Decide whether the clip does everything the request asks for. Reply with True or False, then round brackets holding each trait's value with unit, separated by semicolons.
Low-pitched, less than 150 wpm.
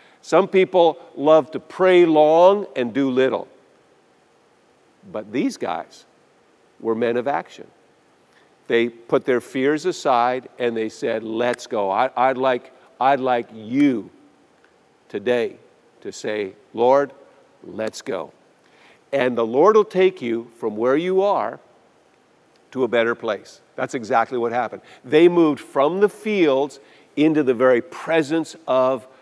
True (130 Hz; 135 wpm)